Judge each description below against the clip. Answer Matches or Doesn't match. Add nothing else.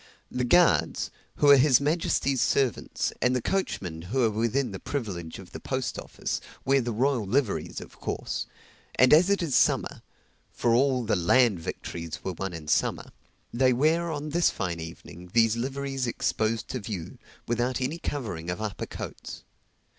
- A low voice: Matches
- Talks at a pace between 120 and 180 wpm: Matches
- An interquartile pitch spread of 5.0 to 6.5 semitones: Matches